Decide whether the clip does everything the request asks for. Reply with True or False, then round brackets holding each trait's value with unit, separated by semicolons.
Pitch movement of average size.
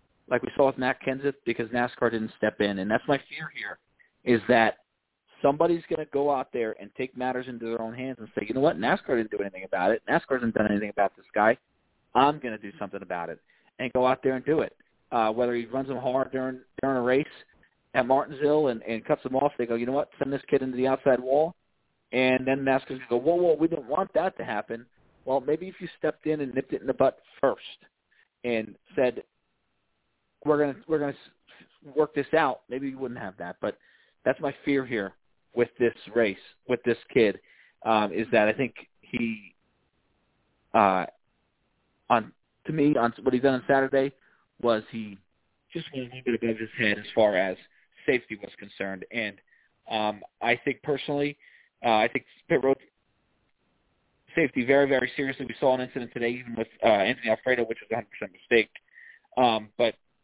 True (3.4 semitones)